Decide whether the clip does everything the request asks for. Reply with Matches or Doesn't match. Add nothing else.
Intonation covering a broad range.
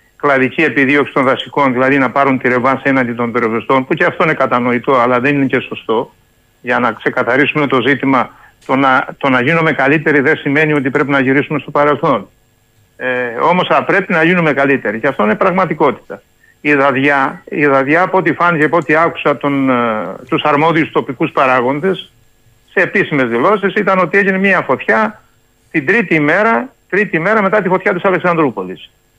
Doesn't match